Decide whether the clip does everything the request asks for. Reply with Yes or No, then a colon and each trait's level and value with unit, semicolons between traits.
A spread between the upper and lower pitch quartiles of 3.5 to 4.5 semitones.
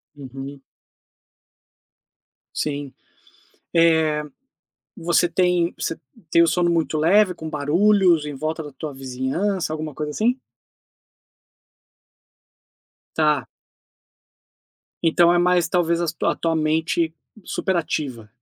No: narrow, 2.6 semitones